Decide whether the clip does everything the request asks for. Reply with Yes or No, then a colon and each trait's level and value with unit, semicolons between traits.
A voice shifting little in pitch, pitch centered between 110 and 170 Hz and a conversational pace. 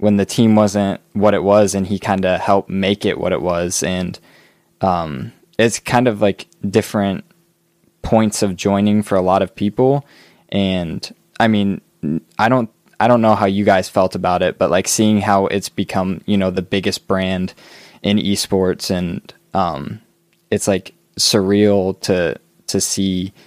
No: narrow, 2.0 semitones; low, 100 Hz; average, 170 wpm